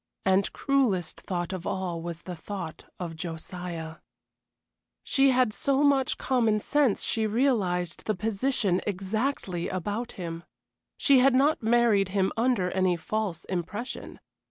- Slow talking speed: Yes, slow, 130 wpm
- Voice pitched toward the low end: No, high, 200 Hz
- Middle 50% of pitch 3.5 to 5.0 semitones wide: No, wide, 5.5 semitones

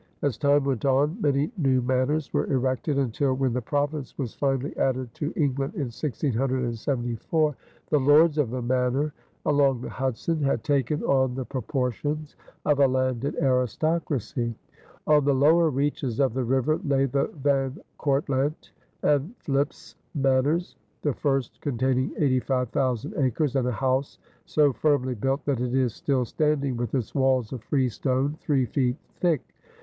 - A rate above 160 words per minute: No, average, 150 wpm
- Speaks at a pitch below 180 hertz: Yes, low, 135 Hz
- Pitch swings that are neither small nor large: No, narrow, 2.2 semitones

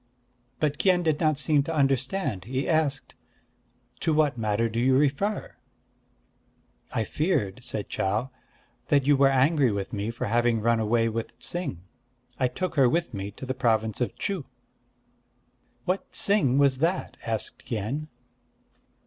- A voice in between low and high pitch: No, low, 130 Hz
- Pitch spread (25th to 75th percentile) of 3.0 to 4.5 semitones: No, average, 5.1 semitones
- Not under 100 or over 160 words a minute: Yes, average, 150 wpm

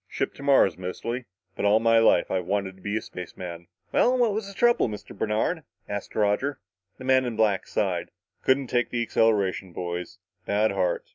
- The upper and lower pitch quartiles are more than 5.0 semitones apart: Yes, wide, 5.5 semitones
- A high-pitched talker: No, low, 110 Hz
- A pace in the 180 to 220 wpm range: Yes, average, 190 wpm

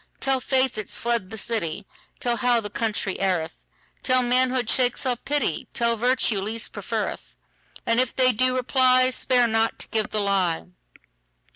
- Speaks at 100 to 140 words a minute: Yes, slow, 135 wpm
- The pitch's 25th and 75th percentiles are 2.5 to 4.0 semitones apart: Yes, average, 3.2 semitones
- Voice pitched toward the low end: No, high, 235 Hz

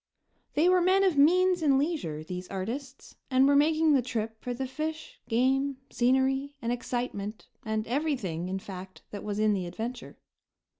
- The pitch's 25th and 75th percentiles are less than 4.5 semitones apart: No, average, 5.3 semitones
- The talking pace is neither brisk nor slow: Yes, average, 165 wpm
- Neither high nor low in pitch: No, very high, 255 Hz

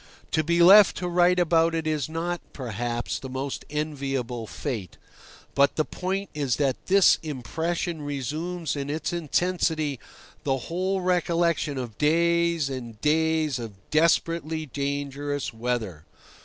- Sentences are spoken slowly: Yes, slow, 130 wpm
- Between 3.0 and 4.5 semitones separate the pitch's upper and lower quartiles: Yes, average, 4.1 semitones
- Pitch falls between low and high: Yes, medium, 155 Hz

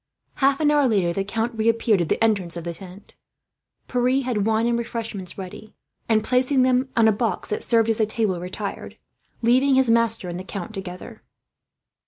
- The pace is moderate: Yes, average, 190 wpm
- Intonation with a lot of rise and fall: No, average, 3.8 semitones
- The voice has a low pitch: No, high, 225 Hz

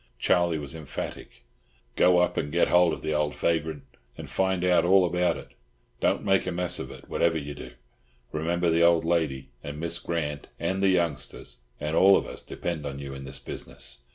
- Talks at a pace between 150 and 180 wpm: No, average, 200 wpm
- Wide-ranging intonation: No, average, 3.1 semitones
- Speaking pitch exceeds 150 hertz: No, very low, 85 Hz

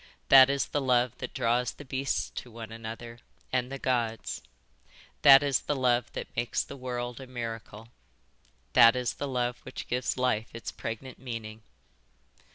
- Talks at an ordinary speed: Yes, average, 165 wpm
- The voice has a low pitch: Yes, low, 125 Hz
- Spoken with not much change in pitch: Yes, narrow, 2.0 semitones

